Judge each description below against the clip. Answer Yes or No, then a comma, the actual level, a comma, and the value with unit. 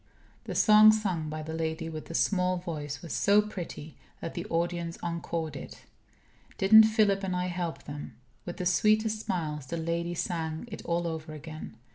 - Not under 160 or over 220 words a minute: Yes, average, 175 wpm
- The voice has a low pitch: No, medium, 170 Hz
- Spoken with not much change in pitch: No, average, 3.3 semitones